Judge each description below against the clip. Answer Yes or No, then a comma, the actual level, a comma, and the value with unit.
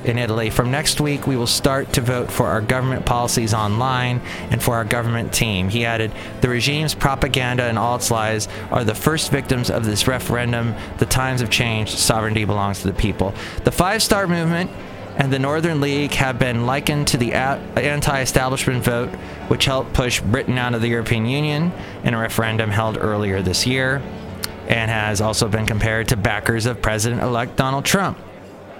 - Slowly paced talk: No, average, 185 wpm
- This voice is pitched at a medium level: No, low, 120 Hz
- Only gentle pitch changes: No, average, 3.3 semitones